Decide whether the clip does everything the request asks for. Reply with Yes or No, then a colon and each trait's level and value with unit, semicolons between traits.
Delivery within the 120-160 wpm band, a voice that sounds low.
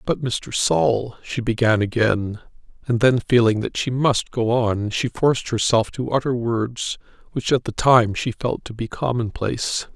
No: average, 175 wpm; low, 120 Hz